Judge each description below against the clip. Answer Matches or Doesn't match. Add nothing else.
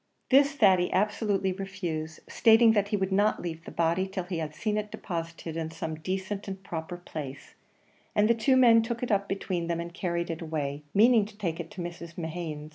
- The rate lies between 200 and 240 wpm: Matches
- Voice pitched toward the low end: Doesn't match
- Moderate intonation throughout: Matches